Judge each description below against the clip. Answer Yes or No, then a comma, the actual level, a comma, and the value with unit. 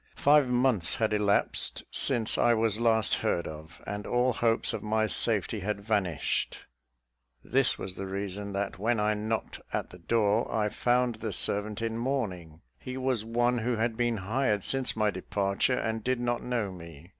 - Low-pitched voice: Yes, low, 110 Hz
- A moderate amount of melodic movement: Yes, average, 3.0 semitones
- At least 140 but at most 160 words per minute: No, average, 175 wpm